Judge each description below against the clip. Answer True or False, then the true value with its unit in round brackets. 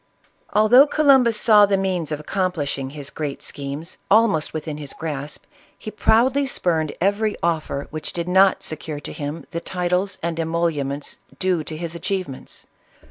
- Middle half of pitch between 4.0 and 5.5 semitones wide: True (4.8 semitones)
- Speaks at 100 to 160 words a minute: True (150 wpm)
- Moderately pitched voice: True (170 Hz)